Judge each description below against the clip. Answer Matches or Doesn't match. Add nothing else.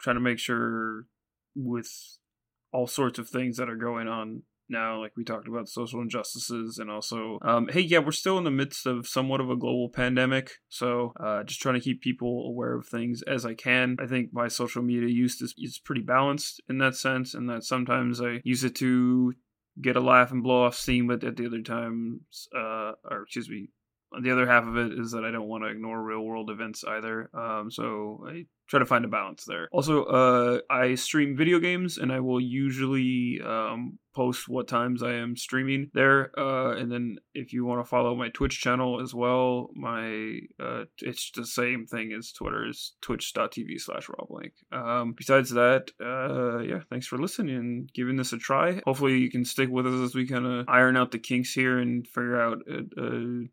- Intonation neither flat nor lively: Doesn't match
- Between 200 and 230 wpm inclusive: Matches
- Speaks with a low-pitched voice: Matches